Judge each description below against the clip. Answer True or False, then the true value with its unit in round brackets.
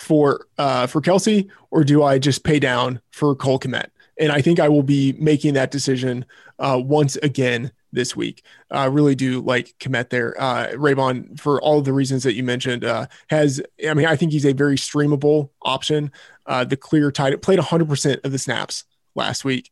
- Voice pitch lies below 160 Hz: True (140 Hz)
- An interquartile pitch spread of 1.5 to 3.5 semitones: True (2.5 semitones)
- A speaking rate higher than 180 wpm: True (200 wpm)